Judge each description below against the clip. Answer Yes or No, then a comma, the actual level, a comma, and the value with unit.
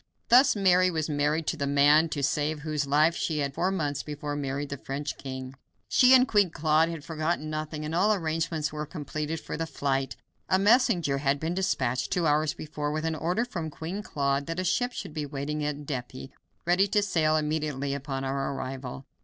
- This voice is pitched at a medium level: Yes, medium, 155 Hz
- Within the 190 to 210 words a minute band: Yes, average, 200 wpm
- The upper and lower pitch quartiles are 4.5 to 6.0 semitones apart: No, average, 2.7 semitones